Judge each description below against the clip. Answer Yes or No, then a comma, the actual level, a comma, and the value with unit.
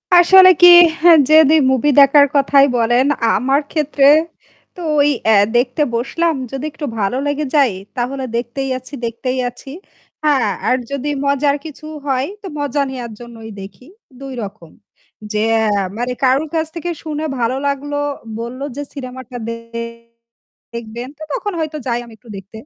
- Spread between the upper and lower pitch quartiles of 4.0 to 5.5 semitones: No, average, 3.6 semitones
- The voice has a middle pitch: No, very high, 270 Hz